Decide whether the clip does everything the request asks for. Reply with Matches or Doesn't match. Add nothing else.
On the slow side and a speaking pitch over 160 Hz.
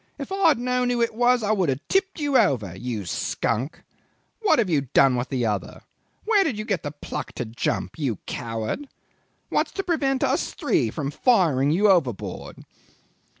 Doesn't match